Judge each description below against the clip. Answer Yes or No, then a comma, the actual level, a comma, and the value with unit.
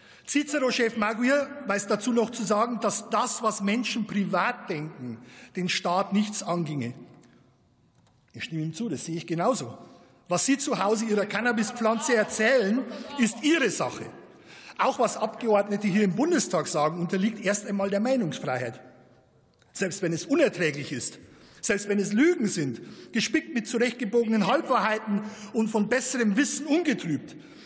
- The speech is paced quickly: No, average, 145 wpm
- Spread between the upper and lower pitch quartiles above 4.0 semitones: Yes, average, 5.0 semitones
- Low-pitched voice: No, high, 215 Hz